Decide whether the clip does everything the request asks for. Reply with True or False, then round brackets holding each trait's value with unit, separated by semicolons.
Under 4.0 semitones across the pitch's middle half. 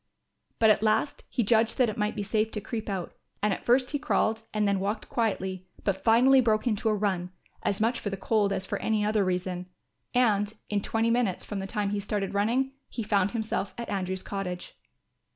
True (2.4 semitones)